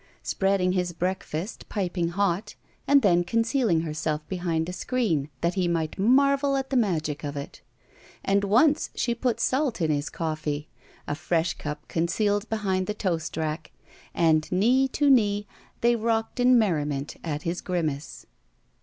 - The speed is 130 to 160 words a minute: Yes, average, 155 wpm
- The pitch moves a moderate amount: No, wide, 5.9 semitones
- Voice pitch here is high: No, medium, 180 Hz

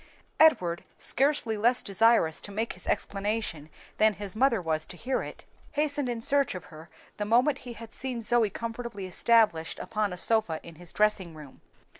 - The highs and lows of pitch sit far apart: No, average, 4.9 semitones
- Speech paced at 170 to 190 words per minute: Yes, average, 175 wpm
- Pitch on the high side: Yes, high, 215 Hz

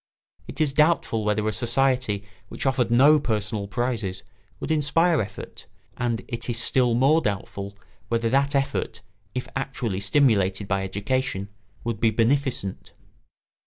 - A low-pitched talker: Yes, low, 120 Hz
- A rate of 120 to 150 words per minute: Yes, slow, 135 wpm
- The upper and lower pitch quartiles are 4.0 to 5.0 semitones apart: Yes, average, 4.7 semitones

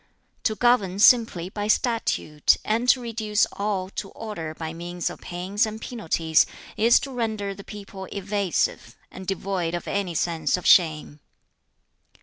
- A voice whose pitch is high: Yes, high, 200 Hz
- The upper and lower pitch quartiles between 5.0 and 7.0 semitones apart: No, average, 3.8 semitones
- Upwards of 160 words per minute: No, average, 145 wpm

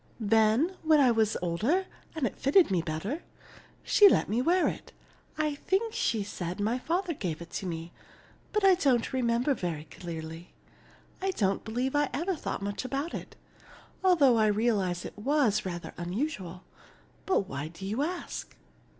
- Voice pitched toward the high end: Yes, high, 230 Hz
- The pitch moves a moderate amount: No, wide, 8.6 semitones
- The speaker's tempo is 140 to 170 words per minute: Yes, average, 160 wpm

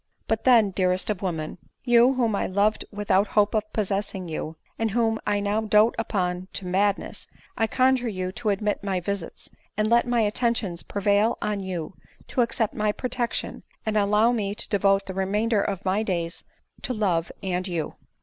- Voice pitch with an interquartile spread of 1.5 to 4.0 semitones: Yes, average, 2.9 semitones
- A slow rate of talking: No, average, 180 wpm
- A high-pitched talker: Yes, high, 205 Hz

